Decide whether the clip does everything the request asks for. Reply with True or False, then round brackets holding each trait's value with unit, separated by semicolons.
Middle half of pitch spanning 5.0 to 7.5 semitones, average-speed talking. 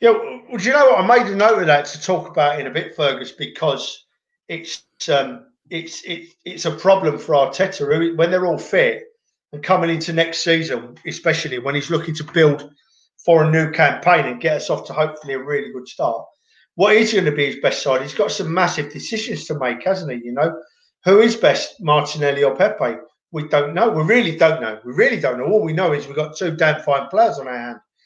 False (5.3 semitones; 230 wpm)